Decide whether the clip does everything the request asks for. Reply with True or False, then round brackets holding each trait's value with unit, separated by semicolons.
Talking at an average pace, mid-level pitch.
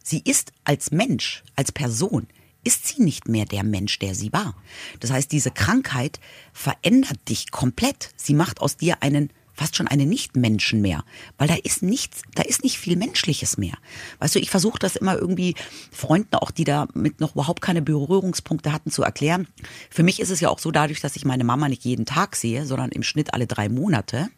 False (200 wpm; 145 Hz)